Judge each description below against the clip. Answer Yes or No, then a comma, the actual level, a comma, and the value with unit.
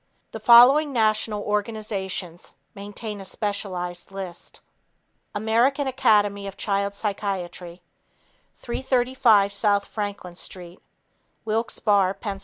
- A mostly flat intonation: Yes, narrow, 2.3 semitones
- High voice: Yes, high, 205 Hz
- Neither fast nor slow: No, slow, 95 wpm